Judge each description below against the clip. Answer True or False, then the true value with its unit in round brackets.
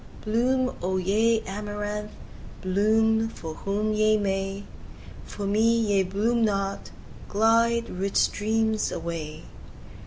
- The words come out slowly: True (105 wpm)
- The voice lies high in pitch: True (210 Hz)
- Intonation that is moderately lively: False (2.2 semitones)